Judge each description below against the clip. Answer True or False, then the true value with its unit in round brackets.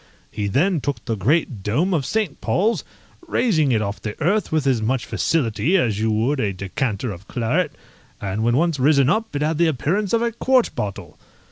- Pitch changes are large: True (7.7 semitones)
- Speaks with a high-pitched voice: False (140 Hz)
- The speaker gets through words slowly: False (200 wpm)